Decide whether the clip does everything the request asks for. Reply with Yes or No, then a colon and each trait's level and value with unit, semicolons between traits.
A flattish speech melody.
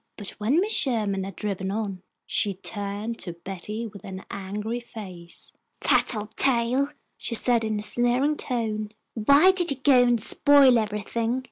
No: average, 3.5 semitones